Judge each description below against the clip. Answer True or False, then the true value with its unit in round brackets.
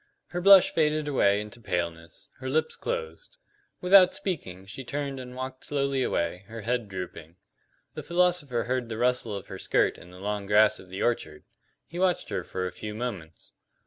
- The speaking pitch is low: True (120 Hz)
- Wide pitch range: True (7.2 semitones)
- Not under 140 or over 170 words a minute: False (180 wpm)